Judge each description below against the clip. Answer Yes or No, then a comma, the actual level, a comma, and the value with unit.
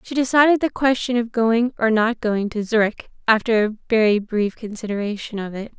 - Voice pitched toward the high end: Yes, high, 225 Hz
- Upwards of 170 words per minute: Yes, average, 185 wpm